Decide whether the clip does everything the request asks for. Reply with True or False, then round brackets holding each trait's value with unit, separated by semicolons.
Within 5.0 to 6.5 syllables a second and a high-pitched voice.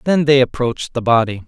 False (5.9 syllables/s; 130 Hz)